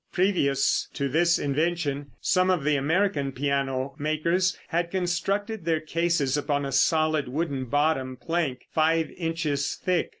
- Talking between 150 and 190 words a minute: No, slow, 135 wpm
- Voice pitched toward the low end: No, medium, 155 Hz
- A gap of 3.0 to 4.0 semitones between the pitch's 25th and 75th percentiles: Yes, average, 3.7 semitones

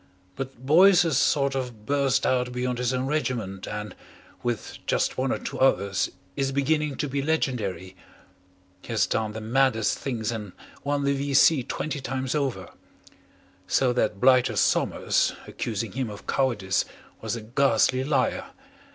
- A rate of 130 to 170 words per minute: Yes, average, 150 wpm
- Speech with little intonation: No, average, 3.7 semitones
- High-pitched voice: No, low, 130 Hz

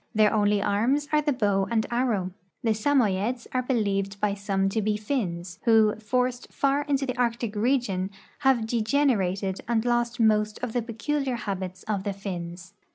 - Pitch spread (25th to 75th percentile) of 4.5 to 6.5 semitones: No, average, 3.8 semitones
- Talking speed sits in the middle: Yes, average, 165 wpm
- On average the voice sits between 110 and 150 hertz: No, high, 220 Hz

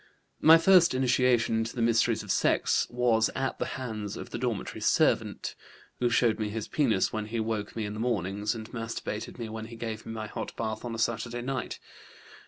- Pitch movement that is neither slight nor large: No, narrow, 1.9 semitones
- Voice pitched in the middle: No, low, 115 Hz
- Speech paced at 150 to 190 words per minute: No, average, 200 wpm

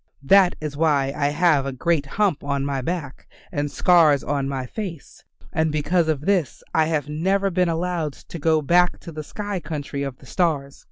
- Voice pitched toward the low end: No, medium, 155 Hz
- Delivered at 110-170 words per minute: No, average, 190 wpm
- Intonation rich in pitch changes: No, average, 3.8 semitones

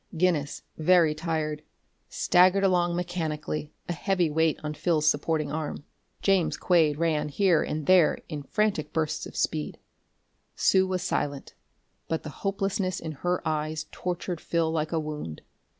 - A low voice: No, medium, 160 Hz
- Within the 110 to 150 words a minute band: Yes, average, 145 wpm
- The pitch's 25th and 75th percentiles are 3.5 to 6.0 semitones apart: No, average, 2.8 semitones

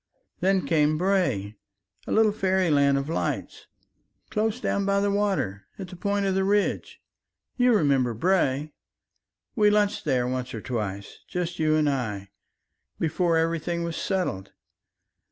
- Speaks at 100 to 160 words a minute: Yes, average, 140 wpm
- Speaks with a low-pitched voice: No, medium, 170 Hz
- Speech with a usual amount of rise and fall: No, wide, 6.6 semitones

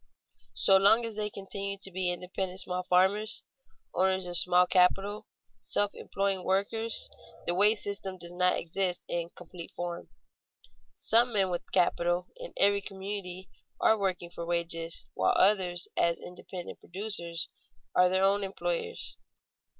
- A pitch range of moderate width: No, narrow, 2.2 semitones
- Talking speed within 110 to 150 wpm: Yes, average, 140 wpm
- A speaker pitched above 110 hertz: Yes, high, 190 Hz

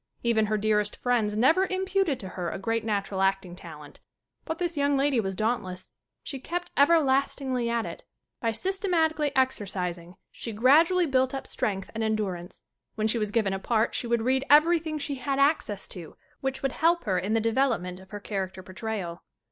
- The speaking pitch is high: Yes, high, 230 Hz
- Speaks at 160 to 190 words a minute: Yes, average, 180 wpm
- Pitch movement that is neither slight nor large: No, wide, 6.3 semitones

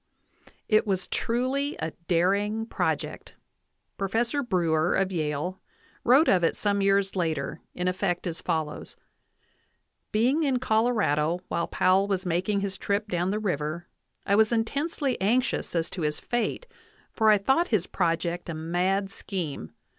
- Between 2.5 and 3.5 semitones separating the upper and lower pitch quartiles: No, average, 4.4 semitones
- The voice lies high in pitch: Yes, high, 195 Hz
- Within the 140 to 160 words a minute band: Yes, average, 145 wpm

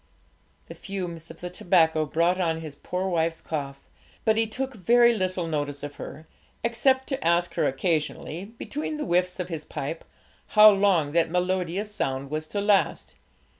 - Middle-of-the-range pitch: Yes, medium, 180 Hz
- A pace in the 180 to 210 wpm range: No, average, 170 wpm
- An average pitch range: Yes, average, 4.2 semitones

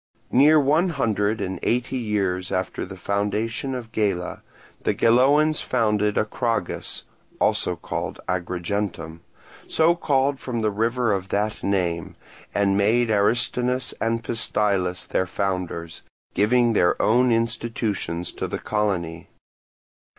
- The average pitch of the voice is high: No, low, 105 Hz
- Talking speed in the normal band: No, slow, 115 wpm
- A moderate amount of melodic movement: Yes, average, 4.1 semitones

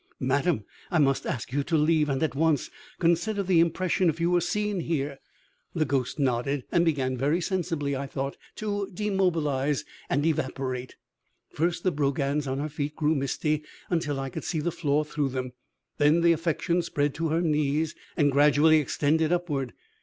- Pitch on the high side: No, medium, 150 Hz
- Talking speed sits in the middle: Yes, average, 175 wpm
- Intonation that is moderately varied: Yes, average, 3.3 semitones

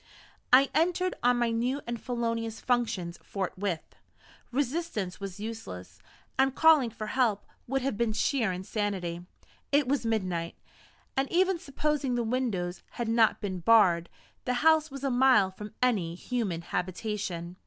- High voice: Yes, high, 230 Hz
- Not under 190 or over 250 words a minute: No, average, 145 wpm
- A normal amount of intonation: No, wide, 5.7 semitones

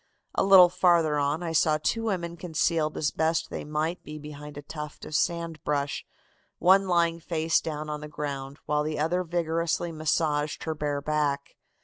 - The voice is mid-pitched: Yes, medium, 155 Hz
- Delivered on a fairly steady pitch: Yes, narrow, 2.1 semitones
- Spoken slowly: No, average, 175 wpm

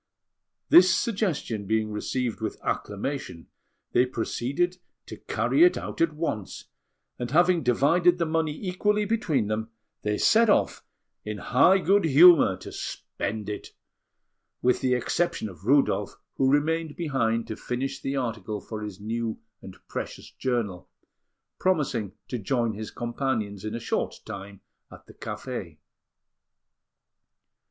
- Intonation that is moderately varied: No, wide, 7.3 semitones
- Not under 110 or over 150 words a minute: Yes, slow, 135 wpm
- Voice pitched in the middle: No, low, 125 Hz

